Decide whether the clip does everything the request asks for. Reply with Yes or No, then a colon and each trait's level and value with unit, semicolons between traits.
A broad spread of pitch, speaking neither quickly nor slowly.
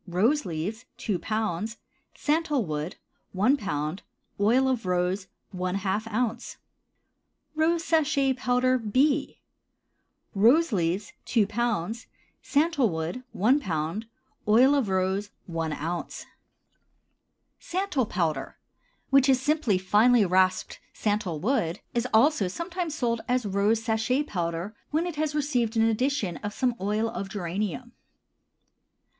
No: wide, 5.9 semitones; slow, 120 wpm